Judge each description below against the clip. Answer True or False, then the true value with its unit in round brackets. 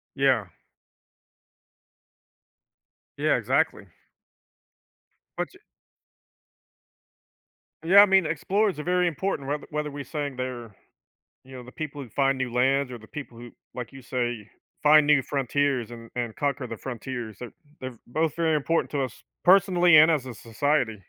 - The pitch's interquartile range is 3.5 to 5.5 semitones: True (4.0 semitones)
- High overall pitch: False (135 Hz)